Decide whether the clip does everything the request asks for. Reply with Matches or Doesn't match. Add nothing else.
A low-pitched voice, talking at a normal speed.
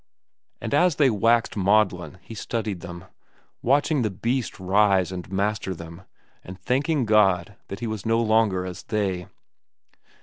Matches